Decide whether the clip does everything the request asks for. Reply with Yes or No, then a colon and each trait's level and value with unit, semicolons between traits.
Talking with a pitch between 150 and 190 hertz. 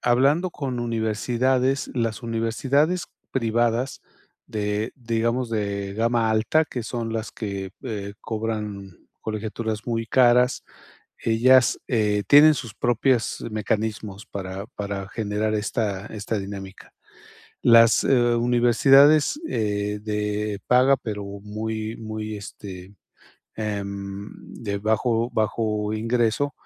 No: low, 110 Hz